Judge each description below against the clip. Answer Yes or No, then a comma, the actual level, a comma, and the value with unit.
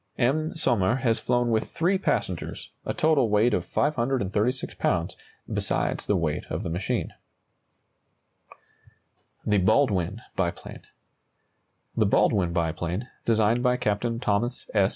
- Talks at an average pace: No, slow, 120 wpm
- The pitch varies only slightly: No, average, 4.7 semitones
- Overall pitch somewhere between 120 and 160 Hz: No, low, 110 Hz